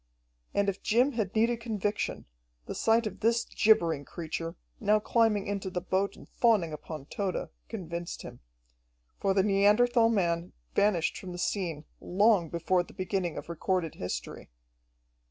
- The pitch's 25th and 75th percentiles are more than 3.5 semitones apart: Yes, average, 4.0 semitones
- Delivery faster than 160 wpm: No, average, 150 wpm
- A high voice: Yes, high, 195 Hz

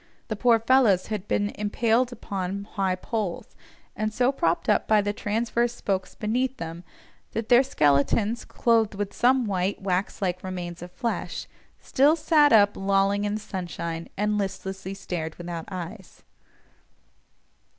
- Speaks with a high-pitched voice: Yes, high, 205 Hz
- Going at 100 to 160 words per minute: Yes, average, 145 wpm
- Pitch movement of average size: Yes, average, 3.7 semitones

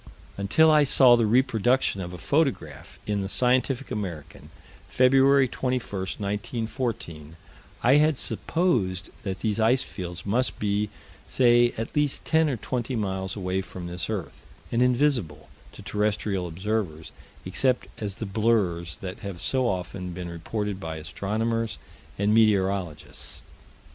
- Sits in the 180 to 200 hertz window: No, low, 105 Hz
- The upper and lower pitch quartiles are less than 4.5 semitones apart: No, average, 5.0 semitones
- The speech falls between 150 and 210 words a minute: No, slow, 135 wpm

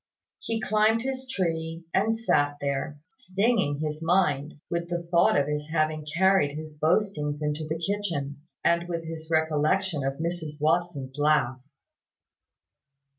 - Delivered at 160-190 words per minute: No, slow, 135 wpm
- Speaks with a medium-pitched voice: Yes, medium, 160 Hz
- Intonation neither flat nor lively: Yes, average, 3.9 semitones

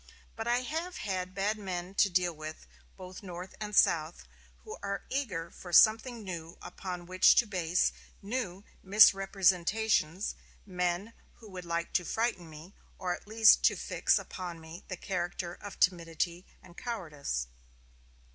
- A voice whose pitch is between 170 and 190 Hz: Yes, medium, 185 Hz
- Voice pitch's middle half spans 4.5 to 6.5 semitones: No, average, 3.3 semitones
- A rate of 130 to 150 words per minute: Yes, average, 145 wpm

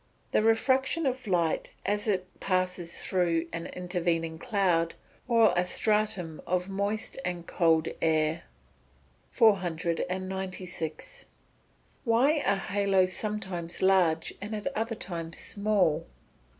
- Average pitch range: Yes, average, 3.8 semitones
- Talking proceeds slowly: Yes, slow, 110 wpm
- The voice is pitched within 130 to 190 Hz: Yes, medium, 185 Hz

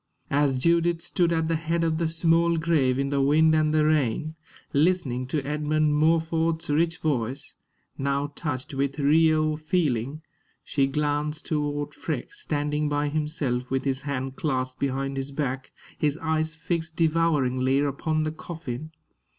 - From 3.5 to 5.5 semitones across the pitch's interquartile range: No, average, 2.7 semitones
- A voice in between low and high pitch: Yes, medium, 150 Hz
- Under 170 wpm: Yes, average, 150 wpm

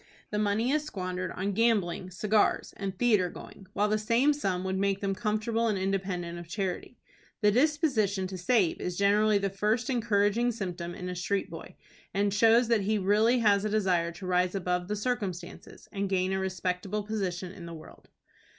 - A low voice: No, high, 200 Hz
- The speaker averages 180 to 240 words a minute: Yes, average, 185 wpm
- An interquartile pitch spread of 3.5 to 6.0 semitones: No, average, 2.8 semitones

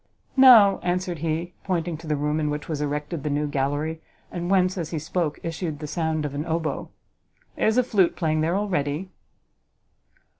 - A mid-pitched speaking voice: Yes, medium, 160 Hz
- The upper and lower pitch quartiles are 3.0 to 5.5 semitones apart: Yes, average, 3.3 semitones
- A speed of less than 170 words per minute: No, average, 185 wpm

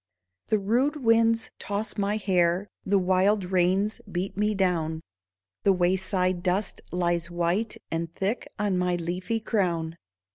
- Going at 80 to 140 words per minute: Yes, slow, 135 wpm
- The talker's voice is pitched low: No, high, 190 Hz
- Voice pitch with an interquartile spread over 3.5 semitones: No, average, 3.0 semitones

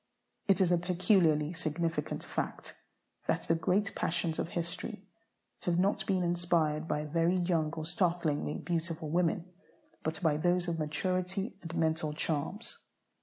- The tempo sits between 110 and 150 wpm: Yes, average, 140 wpm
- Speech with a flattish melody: Yes, narrow, 2.1 semitones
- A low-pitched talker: No, medium, 170 Hz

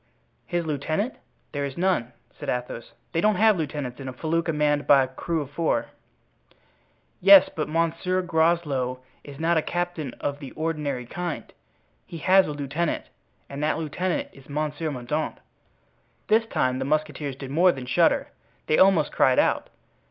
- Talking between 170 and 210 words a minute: No, average, 160 wpm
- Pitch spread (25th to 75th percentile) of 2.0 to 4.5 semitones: Yes, average, 3.7 semitones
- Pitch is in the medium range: Yes, medium, 155 Hz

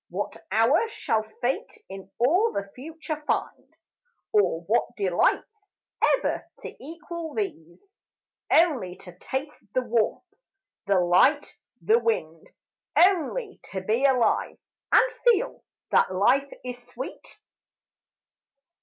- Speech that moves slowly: Yes, slow, 110 wpm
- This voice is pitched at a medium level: No, very high, 275 Hz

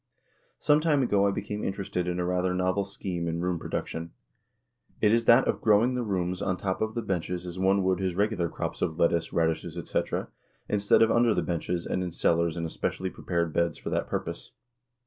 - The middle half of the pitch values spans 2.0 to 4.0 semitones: Yes, average, 3.0 semitones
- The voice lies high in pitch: No, very low, 90 Hz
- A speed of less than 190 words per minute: No, fast, 205 wpm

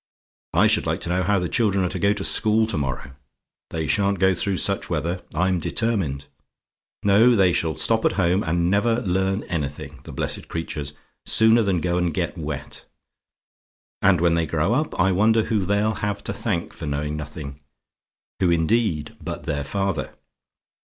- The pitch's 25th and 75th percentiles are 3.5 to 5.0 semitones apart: Yes, average, 4.1 semitones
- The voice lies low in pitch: Yes, very low, 90 Hz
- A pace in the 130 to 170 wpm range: No, average, 180 wpm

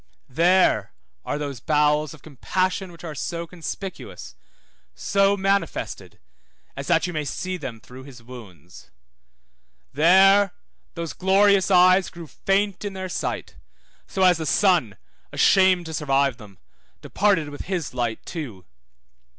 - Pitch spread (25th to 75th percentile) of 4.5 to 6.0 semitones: Yes, average, 5.2 semitones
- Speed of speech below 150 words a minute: Yes, slow, 135 wpm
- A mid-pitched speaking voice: Yes, medium, 170 Hz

